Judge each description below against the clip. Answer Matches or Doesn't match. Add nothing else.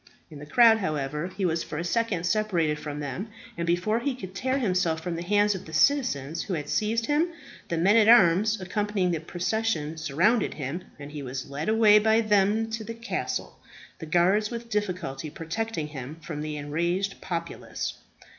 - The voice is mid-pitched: Matches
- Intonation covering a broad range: Matches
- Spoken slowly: Doesn't match